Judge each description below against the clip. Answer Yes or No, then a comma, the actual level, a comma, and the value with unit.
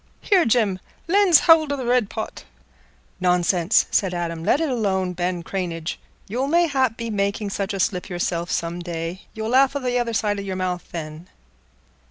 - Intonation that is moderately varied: No, wide, 6.0 semitones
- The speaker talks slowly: No, average, 180 wpm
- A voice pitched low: No, high, 200 Hz